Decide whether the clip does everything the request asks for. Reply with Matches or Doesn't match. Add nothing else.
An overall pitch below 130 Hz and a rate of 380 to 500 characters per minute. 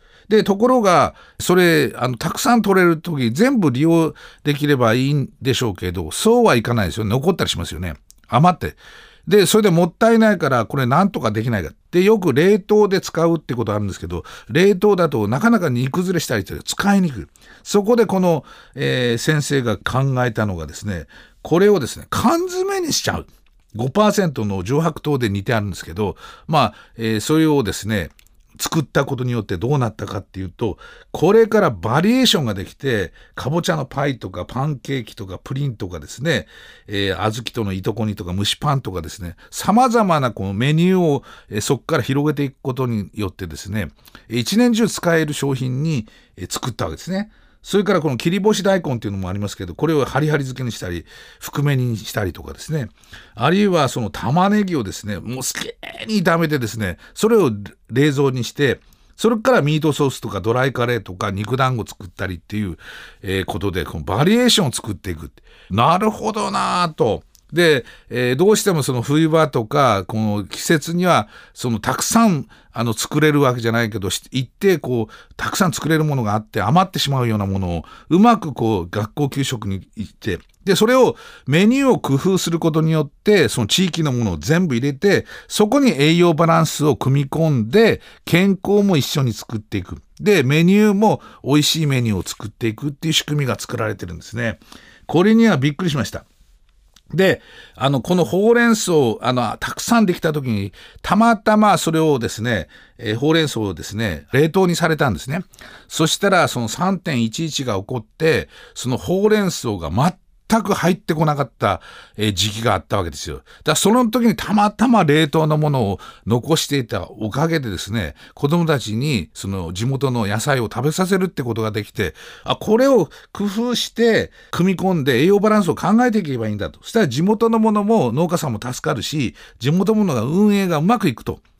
Doesn't match